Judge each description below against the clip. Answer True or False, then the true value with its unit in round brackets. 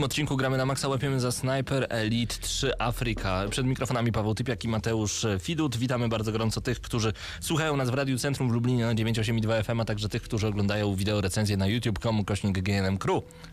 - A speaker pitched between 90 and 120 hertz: True (115 Hz)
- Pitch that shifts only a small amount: False (3.6 semitones)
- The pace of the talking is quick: True (195 wpm)